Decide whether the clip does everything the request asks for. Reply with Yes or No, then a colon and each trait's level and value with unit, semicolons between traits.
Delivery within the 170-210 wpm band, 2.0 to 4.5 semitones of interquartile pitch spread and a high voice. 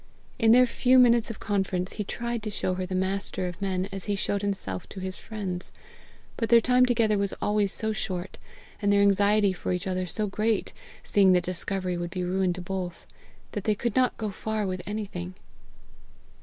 Yes: average, 195 wpm; average, 2.8 semitones; high, 200 Hz